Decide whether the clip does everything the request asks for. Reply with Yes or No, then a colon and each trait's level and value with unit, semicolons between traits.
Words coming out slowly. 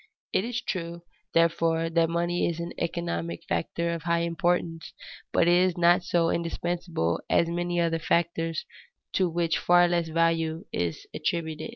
No: average, 155 wpm